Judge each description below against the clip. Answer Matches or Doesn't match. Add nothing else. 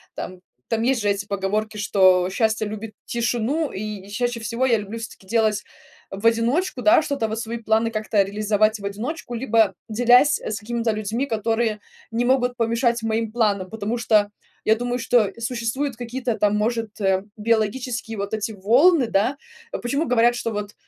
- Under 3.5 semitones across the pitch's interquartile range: Matches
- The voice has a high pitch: Matches